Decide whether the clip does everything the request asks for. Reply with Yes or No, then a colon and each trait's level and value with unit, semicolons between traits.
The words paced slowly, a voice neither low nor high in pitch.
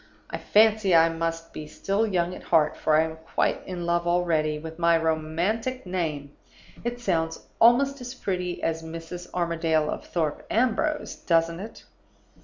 No: average, 160 wpm; medium, 170 Hz